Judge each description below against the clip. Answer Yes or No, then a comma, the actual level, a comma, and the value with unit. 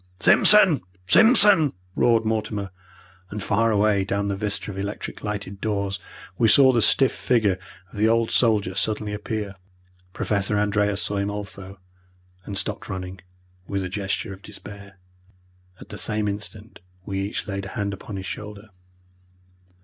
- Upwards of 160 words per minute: No, average, 150 wpm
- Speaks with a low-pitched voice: Yes, low, 105 Hz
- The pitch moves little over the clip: Yes, narrow, 1.6 semitones